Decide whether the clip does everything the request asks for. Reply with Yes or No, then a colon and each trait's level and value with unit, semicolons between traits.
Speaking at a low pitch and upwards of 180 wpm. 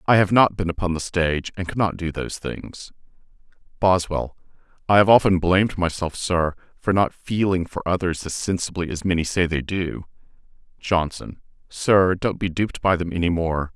No: very low, 90 Hz; average, 175 wpm